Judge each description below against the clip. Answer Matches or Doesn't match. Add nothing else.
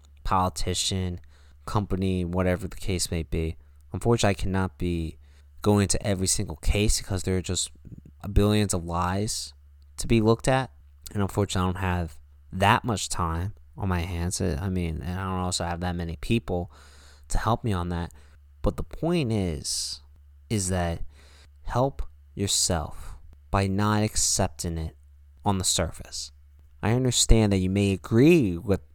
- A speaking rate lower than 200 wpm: Matches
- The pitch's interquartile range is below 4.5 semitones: Doesn't match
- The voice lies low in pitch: Matches